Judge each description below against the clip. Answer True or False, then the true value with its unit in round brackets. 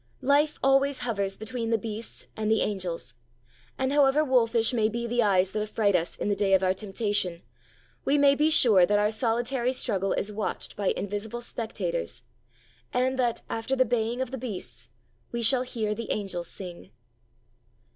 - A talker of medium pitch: False (225 Hz)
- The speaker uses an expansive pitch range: False (3.8 semitones)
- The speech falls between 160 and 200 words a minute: True (175 wpm)